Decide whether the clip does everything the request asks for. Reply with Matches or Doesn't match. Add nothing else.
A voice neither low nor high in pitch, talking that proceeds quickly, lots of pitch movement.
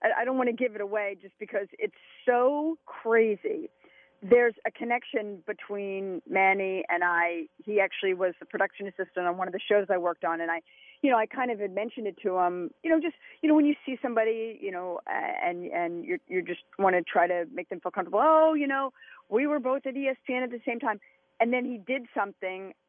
Doesn't match